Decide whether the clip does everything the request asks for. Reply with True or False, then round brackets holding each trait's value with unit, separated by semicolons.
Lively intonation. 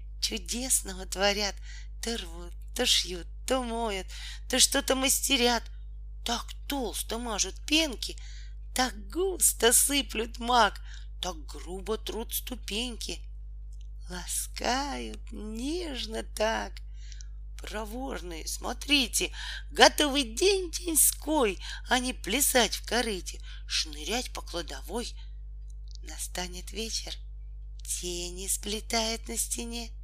True (6.4 semitones)